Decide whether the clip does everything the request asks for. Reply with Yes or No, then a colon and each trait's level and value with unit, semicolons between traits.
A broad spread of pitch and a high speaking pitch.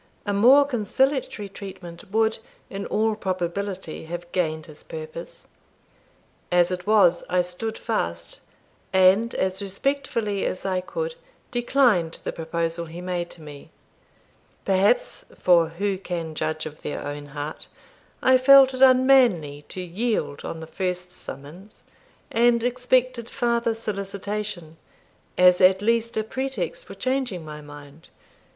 Yes: wide, 5.7 semitones; high, 195 Hz